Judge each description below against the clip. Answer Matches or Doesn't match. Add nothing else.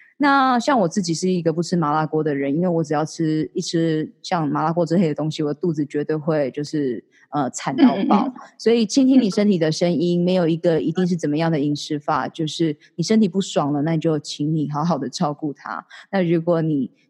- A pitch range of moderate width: Matches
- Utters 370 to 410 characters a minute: Doesn't match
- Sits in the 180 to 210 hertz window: Doesn't match